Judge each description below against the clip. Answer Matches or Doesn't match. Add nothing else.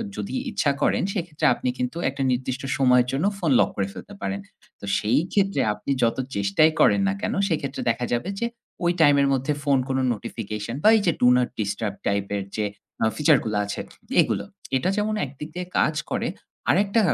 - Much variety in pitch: Matches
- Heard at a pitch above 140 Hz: Doesn't match